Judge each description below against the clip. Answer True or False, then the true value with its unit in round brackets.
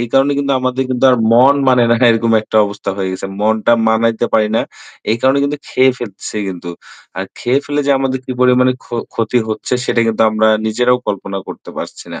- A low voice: True (120 Hz)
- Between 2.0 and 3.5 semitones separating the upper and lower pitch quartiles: True (2.9 semitones)